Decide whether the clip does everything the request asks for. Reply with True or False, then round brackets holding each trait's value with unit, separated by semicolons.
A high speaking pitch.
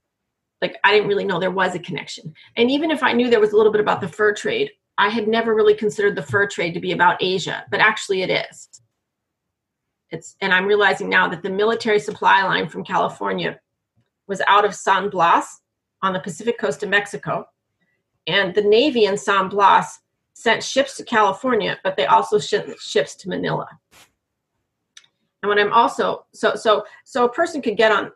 True (205 Hz)